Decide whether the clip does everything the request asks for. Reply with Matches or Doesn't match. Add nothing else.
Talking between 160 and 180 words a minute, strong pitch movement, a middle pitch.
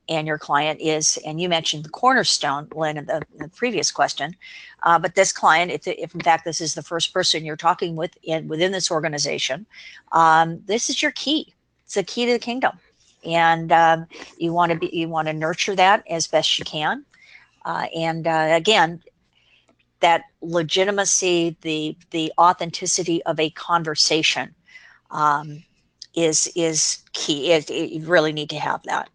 Doesn't match